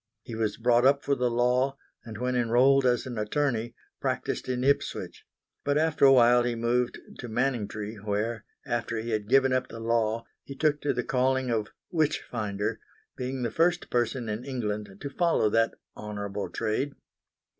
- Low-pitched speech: Yes, low, 120 Hz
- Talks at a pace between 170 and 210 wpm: Yes, average, 175 wpm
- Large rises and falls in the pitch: No, average, 3.2 semitones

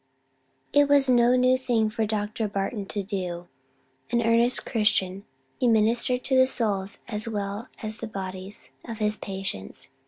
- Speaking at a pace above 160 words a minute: No, average, 155 wpm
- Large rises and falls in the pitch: No, average, 3.4 semitones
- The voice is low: No, high, 215 Hz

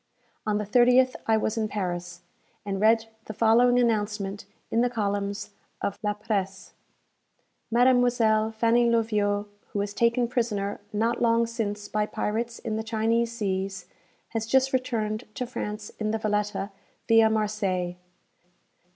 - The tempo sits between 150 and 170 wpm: No, average, 140 wpm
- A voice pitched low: No, high, 220 Hz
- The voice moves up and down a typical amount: No, narrow, 2.2 semitones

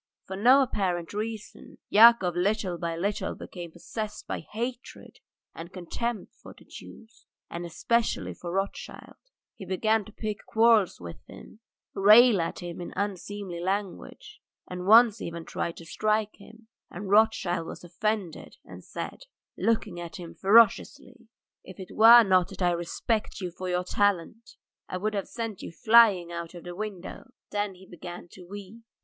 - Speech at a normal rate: Yes, average, 160 wpm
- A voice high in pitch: Yes, high, 200 Hz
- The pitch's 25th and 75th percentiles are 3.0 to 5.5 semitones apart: Yes, average, 3.9 semitones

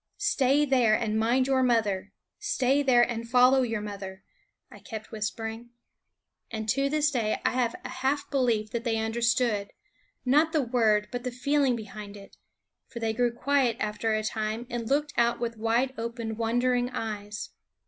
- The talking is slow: No, average, 170 wpm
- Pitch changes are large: No, average, 2.8 semitones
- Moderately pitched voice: No, high, 235 Hz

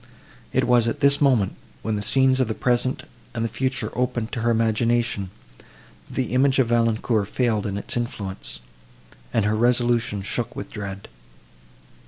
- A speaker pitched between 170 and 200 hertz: No, low, 115 Hz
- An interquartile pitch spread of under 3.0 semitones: Yes, narrow, 2.5 semitones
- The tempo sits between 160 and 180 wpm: Yes, average, 165 wpm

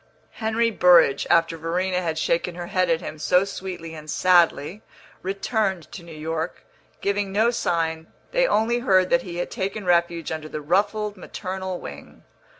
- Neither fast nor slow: Yes, average, 160 wpm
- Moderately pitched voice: Yes, medium, 180 Hz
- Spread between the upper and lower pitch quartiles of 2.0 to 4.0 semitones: Yes, average, 3.1 semitones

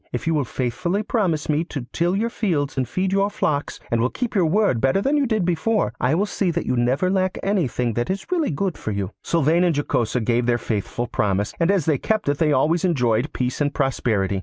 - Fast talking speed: Yes, fast, 235 wpm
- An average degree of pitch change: No, wide, 7.5 semitones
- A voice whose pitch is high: No, medium, 155 Hz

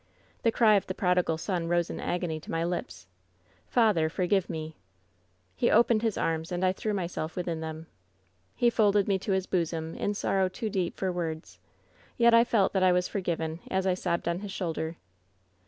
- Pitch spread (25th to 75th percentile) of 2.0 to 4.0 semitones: Yes, average, 3.3 semitones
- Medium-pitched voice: Yes, medium, 180 Hz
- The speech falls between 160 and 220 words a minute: Yes, average, 200 wpm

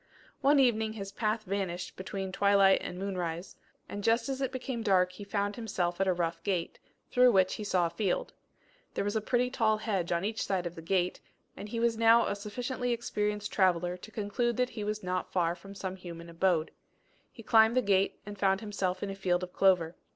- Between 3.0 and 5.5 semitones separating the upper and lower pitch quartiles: Yes, average, 3.3 semitones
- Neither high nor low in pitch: No, high, 200 Hz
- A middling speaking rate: No, fast, 210 wpm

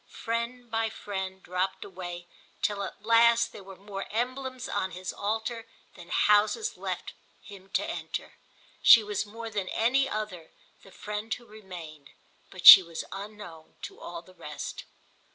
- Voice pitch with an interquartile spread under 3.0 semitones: No, average, 3.6 semitones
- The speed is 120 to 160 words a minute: Yes, average, 150 wpm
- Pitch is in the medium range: No, high, 205 Hz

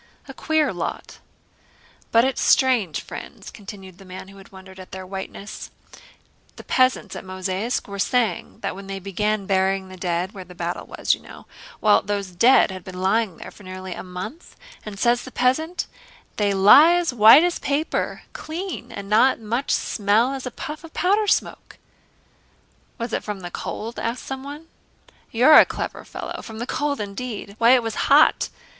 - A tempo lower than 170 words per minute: No, average, 175 wpm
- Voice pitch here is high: Yes, high, 215 Hz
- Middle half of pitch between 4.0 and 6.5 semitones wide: Yes, wide, 5.4 semitones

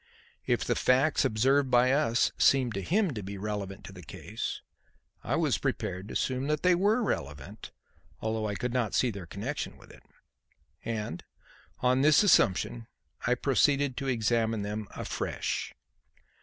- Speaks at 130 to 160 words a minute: Yes, average, 155 wpm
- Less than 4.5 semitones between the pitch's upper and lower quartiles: No, average, 4.9 semitones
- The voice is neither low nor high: No, low, 120 Hz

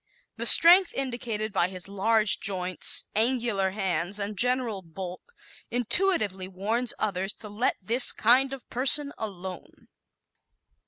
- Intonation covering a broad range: No, average, 4.5 semitones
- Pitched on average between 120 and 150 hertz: No, high, 215 Hz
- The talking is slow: Yes, slow, 120 wpm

